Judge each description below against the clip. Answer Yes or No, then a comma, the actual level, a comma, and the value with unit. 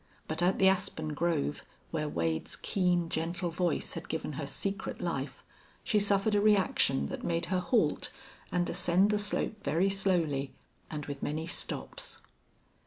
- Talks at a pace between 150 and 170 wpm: Yes, average, 155 wpm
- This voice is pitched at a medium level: Yes, medium, 175 Hz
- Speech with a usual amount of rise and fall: Yes, average, 4.1 semitones